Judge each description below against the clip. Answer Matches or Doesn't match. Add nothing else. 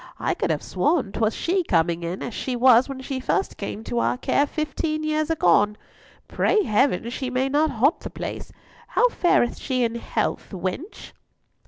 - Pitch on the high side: Matches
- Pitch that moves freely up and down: Matches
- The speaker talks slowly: Doesn't match